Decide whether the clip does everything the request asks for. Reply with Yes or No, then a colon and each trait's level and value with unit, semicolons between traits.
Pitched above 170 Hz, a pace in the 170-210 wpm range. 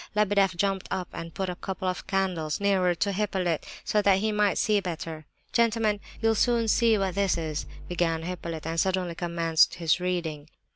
Yes: medium, 185 Hz; average, 180 wpm